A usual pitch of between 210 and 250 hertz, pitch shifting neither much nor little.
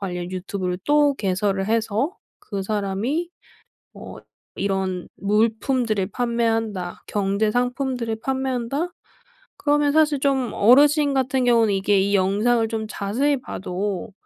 Yes: high, 225 Hz; average, 5.0 semitones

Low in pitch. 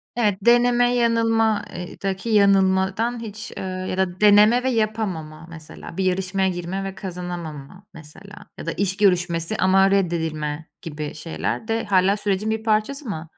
No: high, 195 Hz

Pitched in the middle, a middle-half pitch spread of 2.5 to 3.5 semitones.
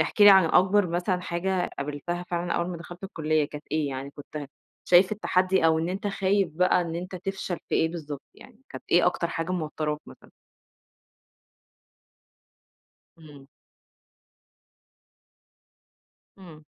Yes: medium, 175 Hz; average, 3.1 semitones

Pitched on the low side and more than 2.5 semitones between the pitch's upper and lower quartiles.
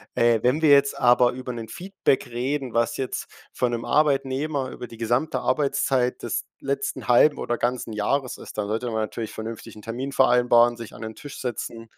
Yes: low, 125 Hz; average, 2.9 semitones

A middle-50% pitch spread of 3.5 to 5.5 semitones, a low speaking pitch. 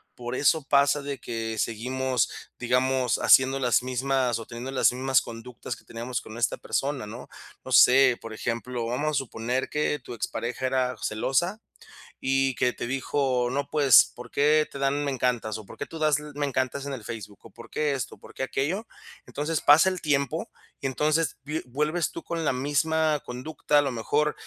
No: average, 3.0 semitones; low, 130 Hz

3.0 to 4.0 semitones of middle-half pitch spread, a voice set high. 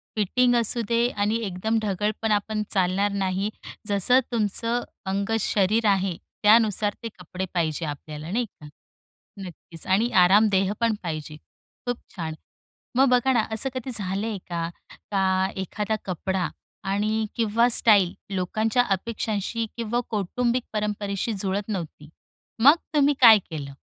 Yes: average, 3.4 semitones; high, 205 Hz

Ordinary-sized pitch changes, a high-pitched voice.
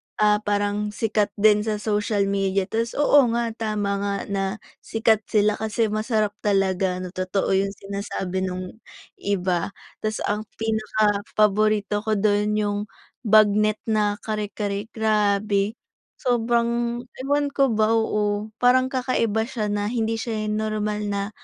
No: narrow, 1.5 semitones; high, 210 Hz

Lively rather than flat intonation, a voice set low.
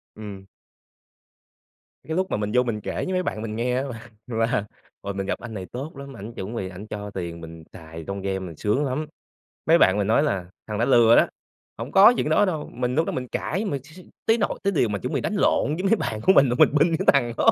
Yes: wide, 6.8 semitones; low, 120 Hz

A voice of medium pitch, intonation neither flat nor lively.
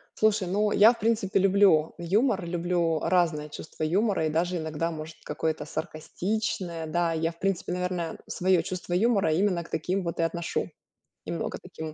Yes: medium, 175 Hz; average, 3.3 semitones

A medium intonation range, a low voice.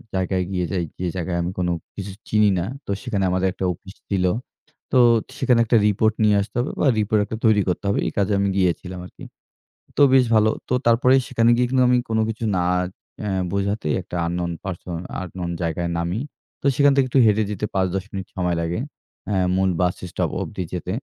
Yes: average, 3.4 semitones; very low, 95 Hz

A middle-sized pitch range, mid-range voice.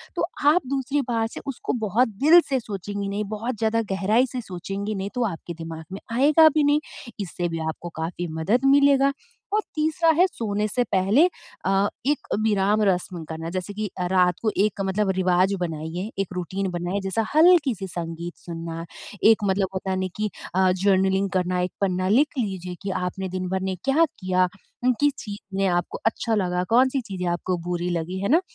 No: average, 4.6 semitones; high, 195 Hz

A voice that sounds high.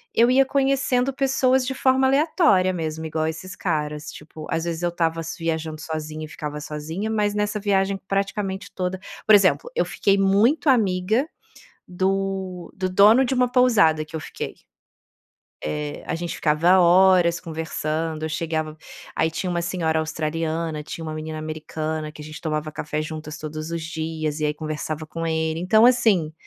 No: medium, 165 Hz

